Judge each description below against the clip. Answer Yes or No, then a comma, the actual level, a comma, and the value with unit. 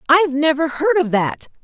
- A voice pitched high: Yes, very high, 300 Hz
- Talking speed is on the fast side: No, average, 185 wpm